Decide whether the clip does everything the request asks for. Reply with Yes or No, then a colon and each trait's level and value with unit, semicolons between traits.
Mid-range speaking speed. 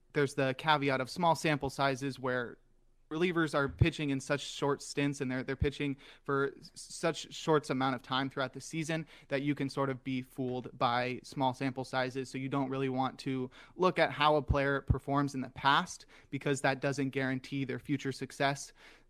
Yes: average, 190 wpm